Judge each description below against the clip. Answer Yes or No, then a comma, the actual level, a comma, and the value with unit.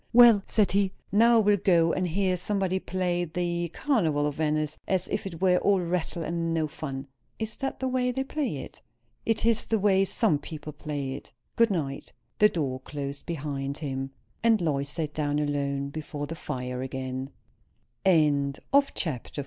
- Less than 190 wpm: Yes, average, 175 wpm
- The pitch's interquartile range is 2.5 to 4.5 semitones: No, average, 5.3 semitones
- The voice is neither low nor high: Yes, medium, 165 Hz